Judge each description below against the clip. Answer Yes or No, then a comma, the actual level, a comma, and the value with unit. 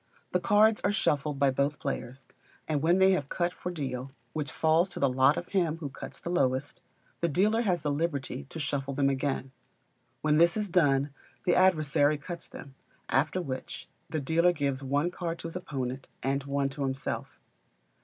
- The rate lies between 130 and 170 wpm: No, average, 185 wpm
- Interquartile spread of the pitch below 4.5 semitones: Yes, average, 4.0 semitones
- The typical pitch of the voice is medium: Yes, medium, 145 Hz